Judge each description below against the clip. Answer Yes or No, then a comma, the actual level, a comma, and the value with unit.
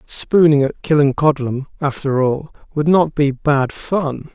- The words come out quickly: No, average, 140 wpm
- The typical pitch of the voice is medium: Yes, medium, 145 Hz